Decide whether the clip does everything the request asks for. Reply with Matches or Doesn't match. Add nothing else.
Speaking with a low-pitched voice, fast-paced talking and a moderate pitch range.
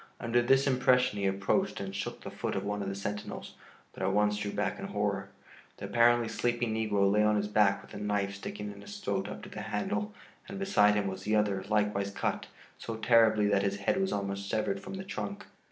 Matches